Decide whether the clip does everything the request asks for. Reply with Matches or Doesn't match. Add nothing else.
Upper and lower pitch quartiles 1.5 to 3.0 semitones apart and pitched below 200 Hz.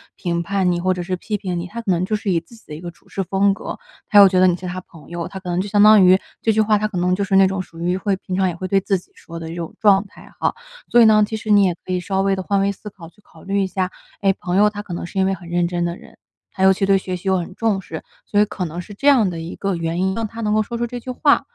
Matches